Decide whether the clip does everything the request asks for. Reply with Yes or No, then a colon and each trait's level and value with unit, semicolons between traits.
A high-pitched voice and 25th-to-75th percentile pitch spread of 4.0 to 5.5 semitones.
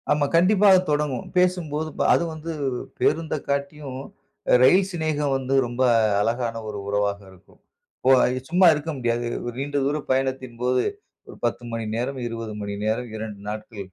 No: low, 130 Hz; average, 4.8 semitones